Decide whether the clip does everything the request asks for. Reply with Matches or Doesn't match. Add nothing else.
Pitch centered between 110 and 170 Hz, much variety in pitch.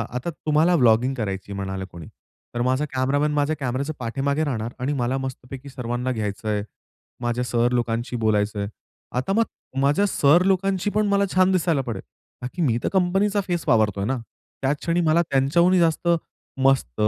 Matches